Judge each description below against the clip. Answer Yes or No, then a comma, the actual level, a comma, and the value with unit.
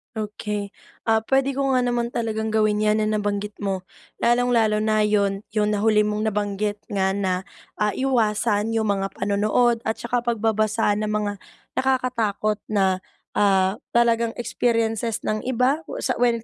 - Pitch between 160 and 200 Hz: No, high, 215 Hz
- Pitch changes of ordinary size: No, narrow, 2.2 semitones